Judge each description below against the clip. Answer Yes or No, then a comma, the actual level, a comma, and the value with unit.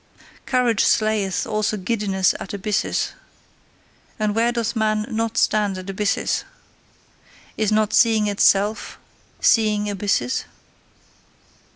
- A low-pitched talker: No, high, 215 Hz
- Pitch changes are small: Yes, narrow, 1.5 semitones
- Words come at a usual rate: No, slow, 100 wpm